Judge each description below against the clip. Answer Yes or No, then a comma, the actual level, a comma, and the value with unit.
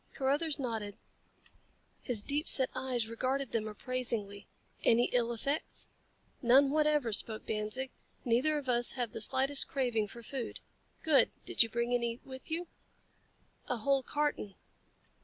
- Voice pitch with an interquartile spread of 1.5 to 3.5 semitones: Yes, average, 3.2 semitones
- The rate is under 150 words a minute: Yes, average, 140 wpm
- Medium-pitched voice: No, very high, 250 Hz